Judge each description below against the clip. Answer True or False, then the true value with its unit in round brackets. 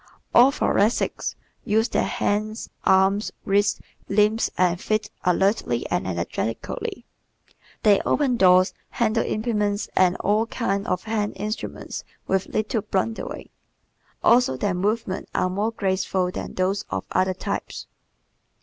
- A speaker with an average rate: False (120 wpm)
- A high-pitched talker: True (205 Hz)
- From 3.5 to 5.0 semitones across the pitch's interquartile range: False (2.7 semitones)